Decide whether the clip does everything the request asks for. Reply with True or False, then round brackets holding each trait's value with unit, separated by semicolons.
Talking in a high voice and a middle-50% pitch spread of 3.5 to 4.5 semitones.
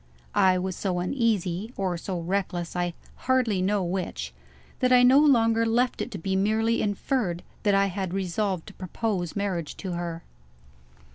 True (195 Hz; 4.0 semitones)